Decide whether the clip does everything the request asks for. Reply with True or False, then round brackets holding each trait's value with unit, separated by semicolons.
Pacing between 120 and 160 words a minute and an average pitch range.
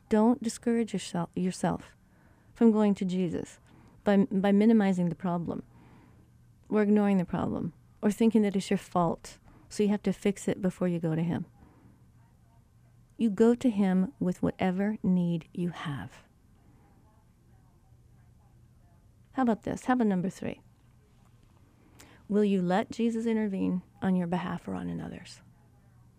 False (135 wpm; 6.2 semitones)